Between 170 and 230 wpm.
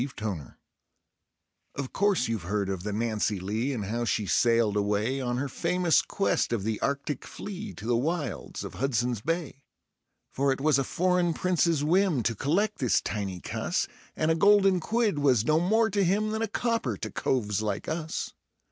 Yes: average, 180 wpm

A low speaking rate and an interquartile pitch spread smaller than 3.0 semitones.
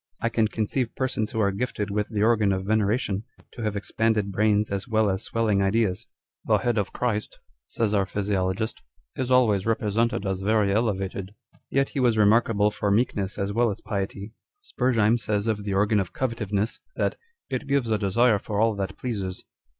No: average, 195 wpm; narrow, 2.4 semitones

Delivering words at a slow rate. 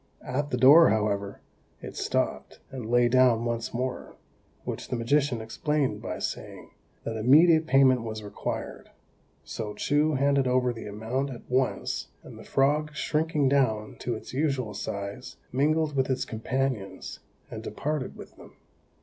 No: average, 150 wpm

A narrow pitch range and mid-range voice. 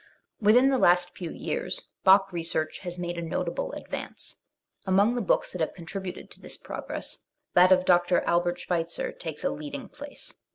Yes: narrow, 2.3 semitones; medium, 180 Hz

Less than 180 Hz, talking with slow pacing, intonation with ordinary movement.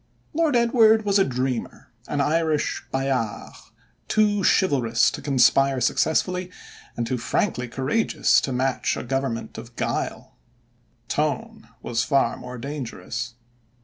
No: low, 135 Hz; slow, 120 wpm; wide, 7.1 semitones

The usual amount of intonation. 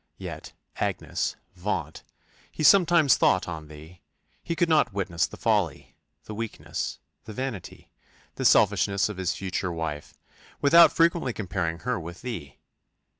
No: wide, 8.4 semitones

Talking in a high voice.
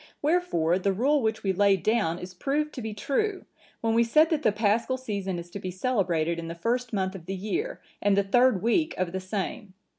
Yes: high, 205 Hz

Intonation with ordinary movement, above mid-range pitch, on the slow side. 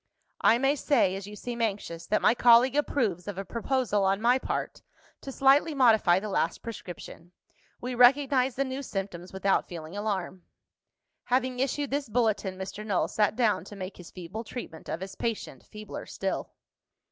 No: average, 4.9 semitones; high, 220 Hz; average, 170 wpm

